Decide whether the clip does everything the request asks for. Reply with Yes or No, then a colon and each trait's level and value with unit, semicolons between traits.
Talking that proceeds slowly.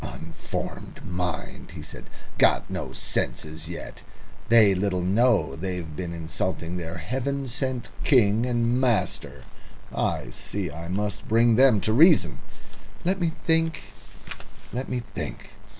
Yes: slow, 130 wpm